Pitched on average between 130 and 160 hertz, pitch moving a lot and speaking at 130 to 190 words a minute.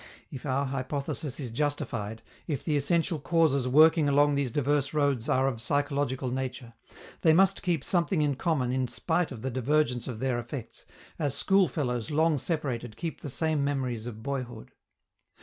No: medium, 140 Hz; average, 3.4 semitones; average, 165 wpm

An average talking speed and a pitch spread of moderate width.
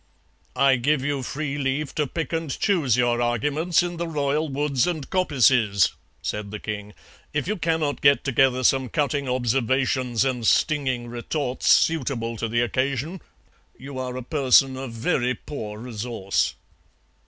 Yes: average, 150 wpm; average, 3.5 semitones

